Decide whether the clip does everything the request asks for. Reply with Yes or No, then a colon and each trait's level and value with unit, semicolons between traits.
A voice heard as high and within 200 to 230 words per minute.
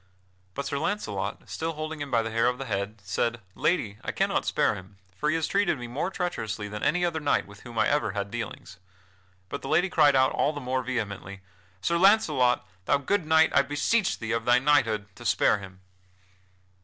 No: low, 130 Hz; fast, 205 wpm